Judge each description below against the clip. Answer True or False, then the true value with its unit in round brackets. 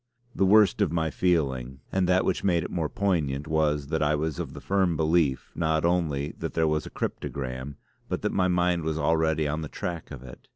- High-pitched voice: False (80 Hz)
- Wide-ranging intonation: False (3.1 semitones)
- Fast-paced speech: True (215 wpm)